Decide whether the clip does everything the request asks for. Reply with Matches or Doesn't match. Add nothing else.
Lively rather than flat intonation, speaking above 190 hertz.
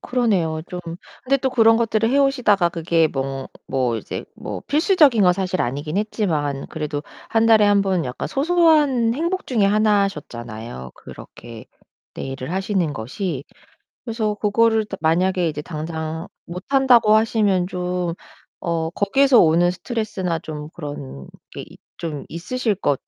Doesn't match